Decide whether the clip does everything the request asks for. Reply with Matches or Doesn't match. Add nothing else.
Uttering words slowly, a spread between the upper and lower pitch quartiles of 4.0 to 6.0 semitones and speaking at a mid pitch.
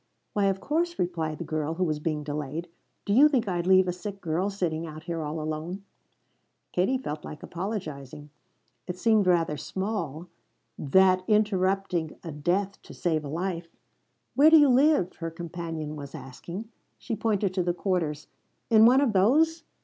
Doesn't match